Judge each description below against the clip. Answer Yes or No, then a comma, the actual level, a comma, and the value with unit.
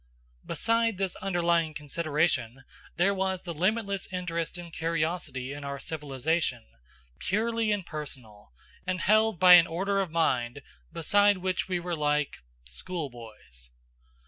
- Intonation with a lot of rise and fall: No, average, 4.5 semitones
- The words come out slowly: Yes, slow, 120 wpm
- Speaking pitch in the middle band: Yes, medium, 170 Hz